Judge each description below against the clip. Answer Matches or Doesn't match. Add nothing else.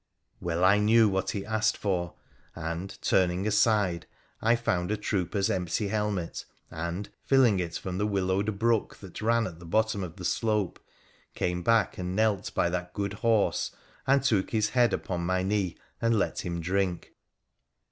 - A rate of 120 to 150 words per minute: Doesn't match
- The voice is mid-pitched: Doesn't match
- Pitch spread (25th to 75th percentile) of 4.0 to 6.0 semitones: Doesn't match